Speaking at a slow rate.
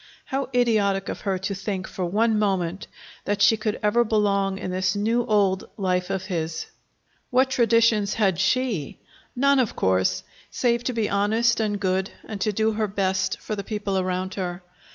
No: average, 175 wpm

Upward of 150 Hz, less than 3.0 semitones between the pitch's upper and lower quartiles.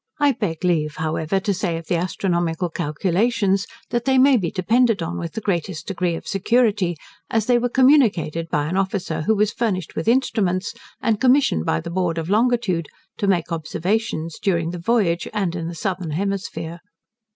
No: medium, 185 Hz; average, 4.8 semitones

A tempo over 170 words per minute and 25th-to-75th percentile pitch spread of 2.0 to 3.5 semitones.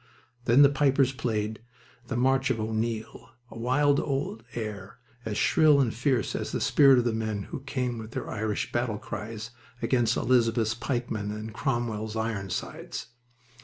No: average, 155 wpm; average, 3.1 semitones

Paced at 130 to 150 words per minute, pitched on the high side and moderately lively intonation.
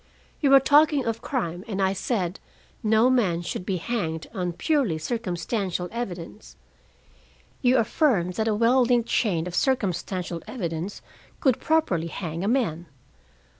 No: average, 140 wpm; high, 205 Hz; wide, 5.9 semitones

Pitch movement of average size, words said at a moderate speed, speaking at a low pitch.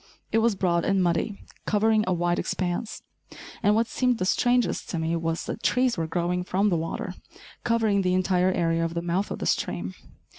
No: average, 4.0 semitones; average, 195 wpm; medium, 185 Hz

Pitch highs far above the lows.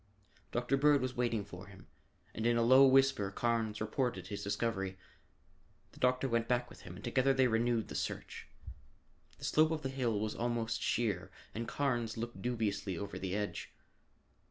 No: average, 3.3 semitones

